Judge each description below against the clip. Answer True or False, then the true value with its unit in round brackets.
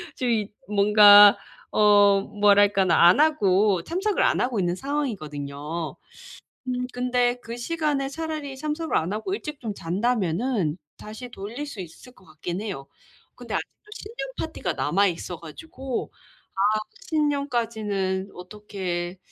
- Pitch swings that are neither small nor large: False (6.0 semitones)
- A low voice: False (210 Hz)